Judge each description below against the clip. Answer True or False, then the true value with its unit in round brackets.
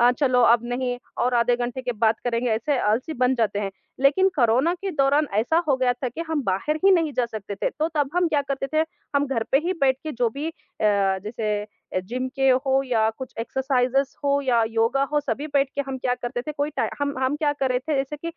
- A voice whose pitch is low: False (260 Hz)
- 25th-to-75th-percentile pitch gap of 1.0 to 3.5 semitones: True (3.2 semitones)